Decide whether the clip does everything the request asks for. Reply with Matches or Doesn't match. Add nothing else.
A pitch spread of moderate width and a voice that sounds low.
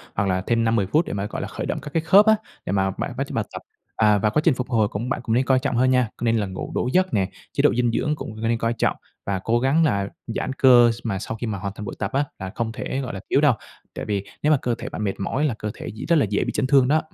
Matches